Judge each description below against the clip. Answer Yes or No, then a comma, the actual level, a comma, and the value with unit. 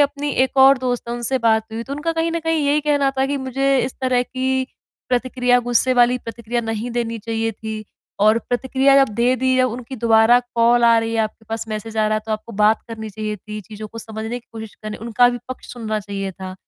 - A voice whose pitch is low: No, high, 235 Hz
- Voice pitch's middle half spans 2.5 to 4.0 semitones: Yes, average, 2.8 semitones